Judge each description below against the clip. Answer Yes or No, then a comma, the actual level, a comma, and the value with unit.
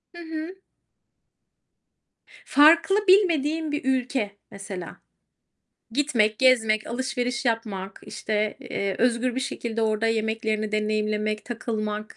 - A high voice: Yes, high, 230 Hz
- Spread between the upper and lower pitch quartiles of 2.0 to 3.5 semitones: No, average, 4.1 semitones